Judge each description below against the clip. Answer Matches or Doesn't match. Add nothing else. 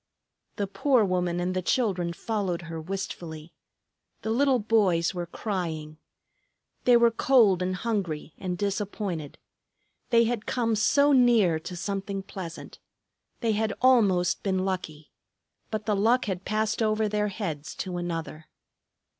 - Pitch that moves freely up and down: Doesn't match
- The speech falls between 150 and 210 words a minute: Doesn't match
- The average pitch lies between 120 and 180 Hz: Doesn't match